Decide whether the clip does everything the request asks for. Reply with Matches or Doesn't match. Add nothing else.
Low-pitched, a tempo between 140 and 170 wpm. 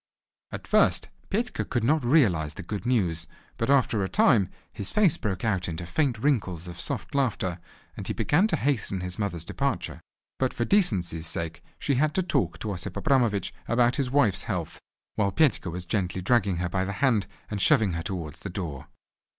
Doesn't match